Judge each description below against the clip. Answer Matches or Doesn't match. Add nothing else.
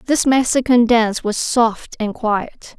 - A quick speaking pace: Doesn't match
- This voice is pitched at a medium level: Doesn't match